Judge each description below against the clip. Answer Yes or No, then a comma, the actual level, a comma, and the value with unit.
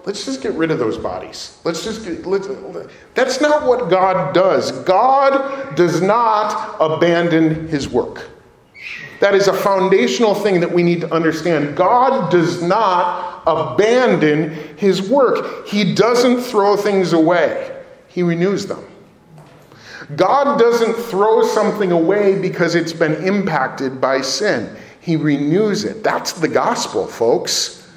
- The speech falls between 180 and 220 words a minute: No, average, 140 wpm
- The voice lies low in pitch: No, high, 195 Hz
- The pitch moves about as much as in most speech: No, wide, 5.8 semitones